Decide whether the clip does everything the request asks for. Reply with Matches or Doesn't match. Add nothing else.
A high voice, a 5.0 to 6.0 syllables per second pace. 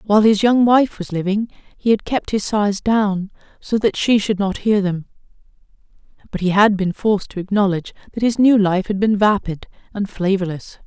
Matches